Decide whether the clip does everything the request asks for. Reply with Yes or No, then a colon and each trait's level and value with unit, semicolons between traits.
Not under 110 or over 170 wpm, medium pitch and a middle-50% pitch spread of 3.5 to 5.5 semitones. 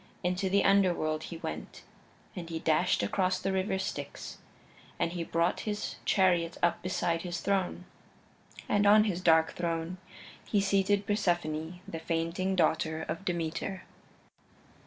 No: slow, 135 wpm; medium, 175 Hz; narrow, 2.5 semitones